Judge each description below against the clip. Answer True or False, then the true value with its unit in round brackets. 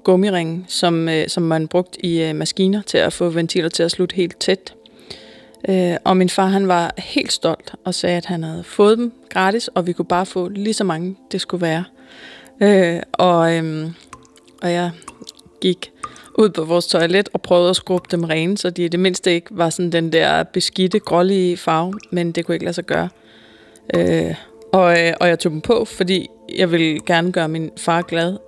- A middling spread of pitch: False (2.1 semitones)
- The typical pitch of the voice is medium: True (175 Hz)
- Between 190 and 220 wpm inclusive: True (205 wpm)